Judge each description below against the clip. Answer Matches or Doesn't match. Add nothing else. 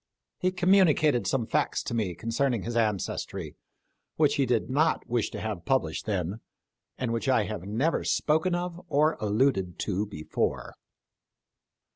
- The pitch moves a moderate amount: Doesn't match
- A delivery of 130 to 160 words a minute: Matches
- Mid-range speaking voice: Doesn't match